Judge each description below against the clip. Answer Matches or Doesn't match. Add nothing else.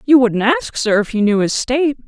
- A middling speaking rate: Doesn't match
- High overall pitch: Matches